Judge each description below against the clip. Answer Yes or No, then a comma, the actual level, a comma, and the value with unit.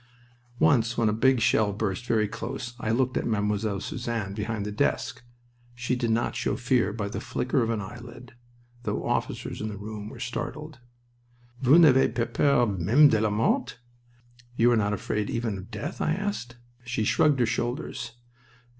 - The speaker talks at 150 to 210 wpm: Yes, average, 175 wpm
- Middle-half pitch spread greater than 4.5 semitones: No, average, 2.7 semitones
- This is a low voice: Yes, low, 115 Hz